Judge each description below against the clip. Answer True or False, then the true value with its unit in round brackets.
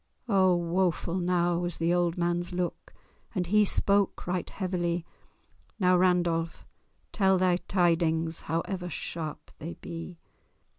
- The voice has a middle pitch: True (175 Hz)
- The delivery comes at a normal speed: False (120 wpm)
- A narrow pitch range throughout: True (1.5 semitones)